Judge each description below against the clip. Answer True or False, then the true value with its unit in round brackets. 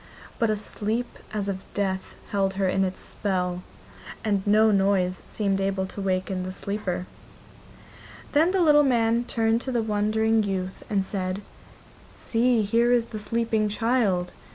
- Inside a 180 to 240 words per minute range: False (155 wpm)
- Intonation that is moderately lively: True (3.0 semitones)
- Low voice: False (210 Hz)